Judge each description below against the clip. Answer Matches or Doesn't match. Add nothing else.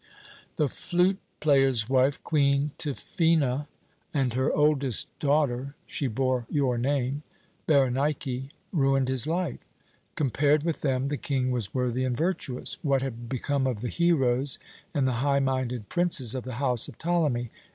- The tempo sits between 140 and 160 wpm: Matches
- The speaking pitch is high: Doesn't match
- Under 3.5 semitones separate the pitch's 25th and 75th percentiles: Matches